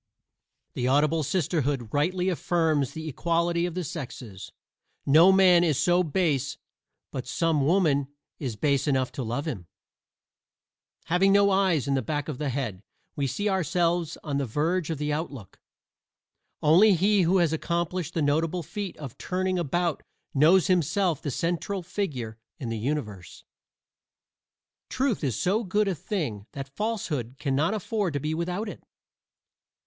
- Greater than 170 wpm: No, average, 155 wpm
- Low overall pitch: No, medium, 160 Hz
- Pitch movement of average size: Yes, average, 4.6 semitones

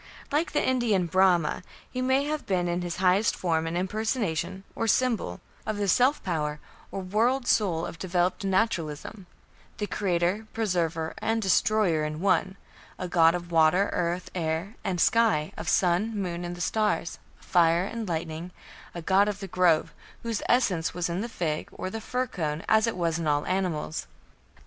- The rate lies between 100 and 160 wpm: No, average, 170 wpm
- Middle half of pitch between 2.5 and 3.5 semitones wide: No, average, 4.3 semitones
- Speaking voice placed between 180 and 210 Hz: Yes, medium, 185 Hz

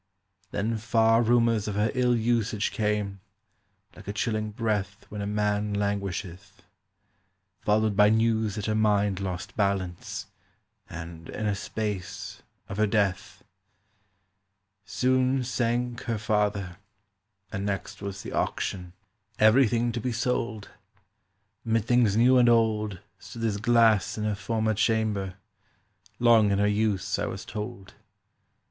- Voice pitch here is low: Yes, low, 105 Hz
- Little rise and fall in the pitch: Yes, narrow, 2.2 semitones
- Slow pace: Yes, slow, 130 wpm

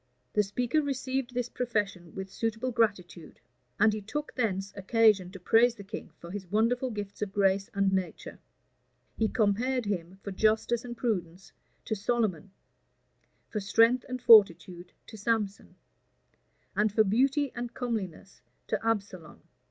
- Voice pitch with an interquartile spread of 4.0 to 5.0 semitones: No, average, 3.6 semitones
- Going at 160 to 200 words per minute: No, average, 145 wpm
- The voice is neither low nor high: No, high, 210 Hz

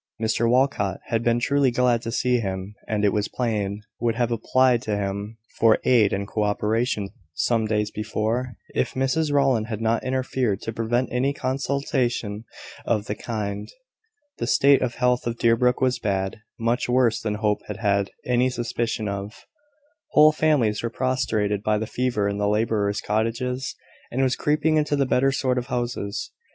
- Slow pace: No, average, 175 wpm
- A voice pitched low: Yes, low, 115 Hz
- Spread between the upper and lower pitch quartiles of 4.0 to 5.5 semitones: No, average, 3.3 semitones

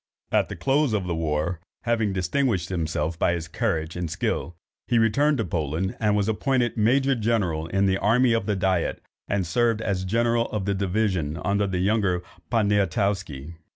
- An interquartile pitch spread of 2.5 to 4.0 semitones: No, average, 4.5 semitones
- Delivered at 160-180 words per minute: Yes, average, 165 wpm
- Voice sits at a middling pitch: No, low, 100 Hz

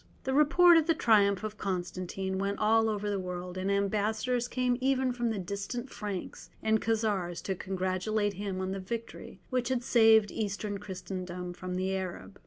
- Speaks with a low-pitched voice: No, high, 205 Hz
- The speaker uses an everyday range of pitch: Yes, average, 3.3 semitones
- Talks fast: No, average, 175 wpm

